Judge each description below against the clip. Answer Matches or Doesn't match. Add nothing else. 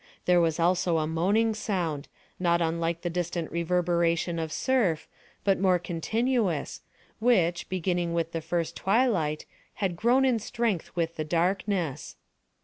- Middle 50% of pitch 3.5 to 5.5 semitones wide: Doesn't match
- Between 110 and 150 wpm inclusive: Matches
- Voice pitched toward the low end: Doesn't match